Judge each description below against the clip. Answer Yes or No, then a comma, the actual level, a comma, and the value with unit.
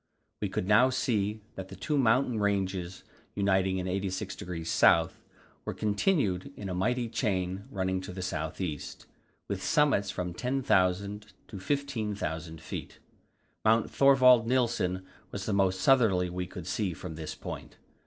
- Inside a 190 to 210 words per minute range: No, average, 145 wpm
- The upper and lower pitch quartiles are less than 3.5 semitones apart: No, average, 3.9 semitones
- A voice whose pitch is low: Yes, low, 100 Hz